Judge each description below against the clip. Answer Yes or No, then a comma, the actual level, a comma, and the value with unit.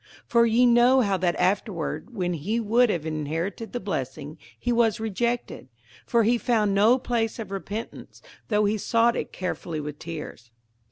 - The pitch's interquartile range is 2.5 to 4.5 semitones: No, wide, 5.4 semitones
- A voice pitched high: Yes, high, 210 Hz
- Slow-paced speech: No, average, 170 wpm